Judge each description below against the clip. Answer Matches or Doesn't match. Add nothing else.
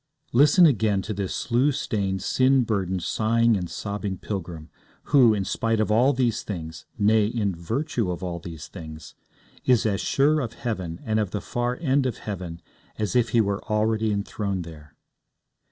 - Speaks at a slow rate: Doesn't match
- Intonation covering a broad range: Doesn't match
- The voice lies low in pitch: Matches